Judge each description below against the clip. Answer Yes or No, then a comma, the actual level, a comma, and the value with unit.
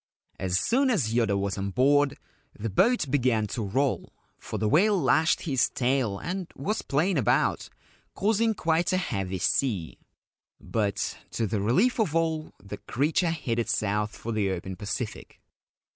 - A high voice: No, low, 130 Hz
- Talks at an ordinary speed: Yes, average, 155 wpm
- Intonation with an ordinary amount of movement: No, wide, 8.0 semitones